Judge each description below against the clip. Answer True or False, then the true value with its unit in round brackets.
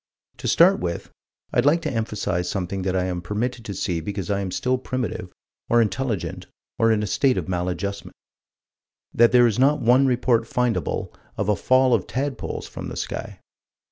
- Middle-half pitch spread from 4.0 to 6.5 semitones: True (4.9 semitones)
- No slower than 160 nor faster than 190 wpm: True (180 wpm)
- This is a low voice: True (110 Hz)